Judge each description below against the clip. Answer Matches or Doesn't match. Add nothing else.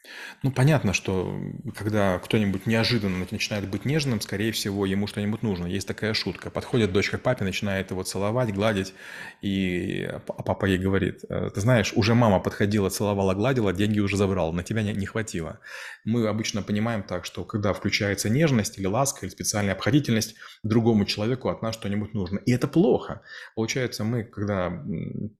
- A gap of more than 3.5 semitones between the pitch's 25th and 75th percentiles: Doesn't match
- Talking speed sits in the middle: Doesn't match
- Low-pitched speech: Matches